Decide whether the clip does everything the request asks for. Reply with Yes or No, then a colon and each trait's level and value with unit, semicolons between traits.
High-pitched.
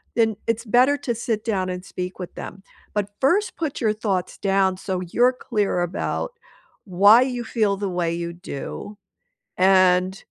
Yes: high, 200 Hz